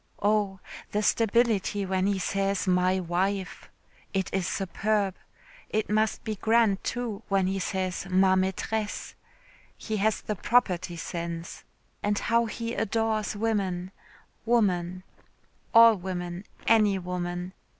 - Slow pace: Yes, slow, 120 wpm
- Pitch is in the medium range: No, high, 195 Hz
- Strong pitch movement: No, average, 2.8 semitones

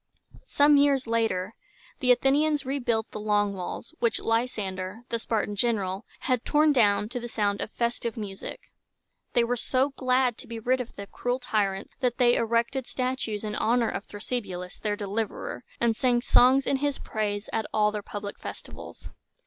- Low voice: No, high, 230 Hz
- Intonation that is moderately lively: Yes, average, 3.4 semitones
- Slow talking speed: No, average, 175 wpm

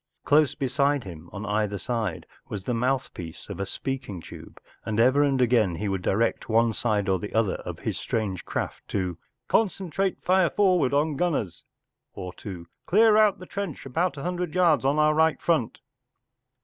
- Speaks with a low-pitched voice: Yes, low, 130 Hz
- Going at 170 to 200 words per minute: Yes, average, 175 wpm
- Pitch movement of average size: No, wide, 7.8 semitones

